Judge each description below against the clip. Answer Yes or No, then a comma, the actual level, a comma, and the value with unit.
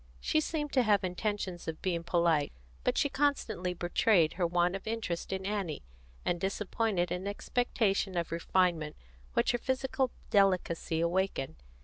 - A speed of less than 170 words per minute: Yes, average, 145 wpm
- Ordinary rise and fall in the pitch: Yes, average, 3.9 semitones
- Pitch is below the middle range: No, medium, 185 Hz